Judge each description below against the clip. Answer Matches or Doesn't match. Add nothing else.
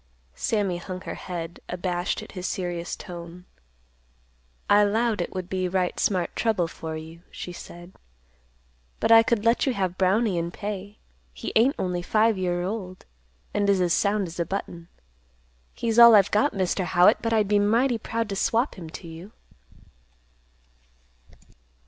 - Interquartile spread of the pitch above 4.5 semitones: Doesn't match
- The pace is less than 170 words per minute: Matches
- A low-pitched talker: Doesn't match